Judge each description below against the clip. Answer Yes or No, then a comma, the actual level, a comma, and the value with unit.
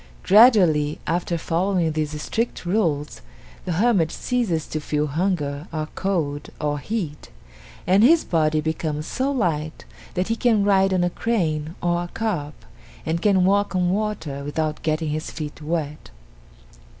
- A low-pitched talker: No, medium, 170 Hz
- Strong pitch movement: No, average, 4.4 semitones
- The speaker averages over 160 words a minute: No, average, 150 wpm